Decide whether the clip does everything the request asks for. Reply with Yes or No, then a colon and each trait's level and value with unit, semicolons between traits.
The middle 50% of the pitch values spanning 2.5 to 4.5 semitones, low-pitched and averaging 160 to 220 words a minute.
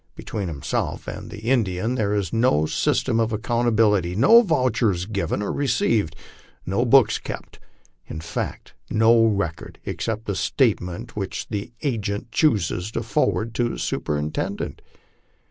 No: average, 3.7 semitones; low, 110 Hz; slow, 135 wpm